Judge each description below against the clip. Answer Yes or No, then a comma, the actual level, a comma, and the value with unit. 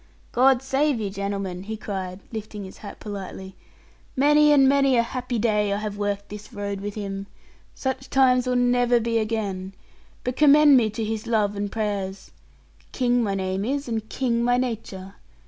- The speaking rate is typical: Yes, average, 175 wpm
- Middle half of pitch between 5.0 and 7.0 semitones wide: No, average, 3.9 semitones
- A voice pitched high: Yes, high, 220 Hz